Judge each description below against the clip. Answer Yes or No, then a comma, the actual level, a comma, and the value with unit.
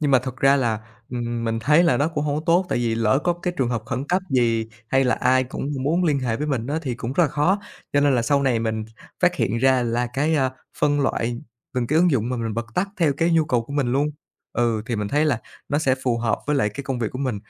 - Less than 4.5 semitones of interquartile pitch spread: Yes, average, 3.9 semitones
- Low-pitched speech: Yes, low, 130 Hz